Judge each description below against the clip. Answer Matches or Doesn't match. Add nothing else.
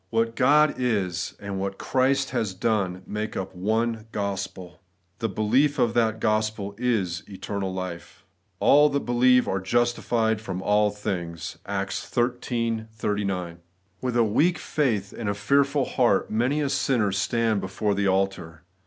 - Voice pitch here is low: Matches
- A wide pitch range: Doesn't match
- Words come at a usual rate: Matches